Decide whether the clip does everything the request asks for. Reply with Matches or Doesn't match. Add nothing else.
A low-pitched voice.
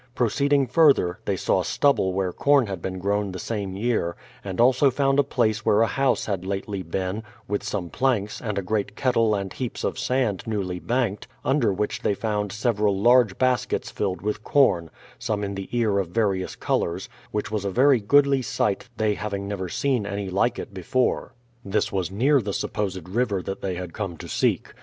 Matches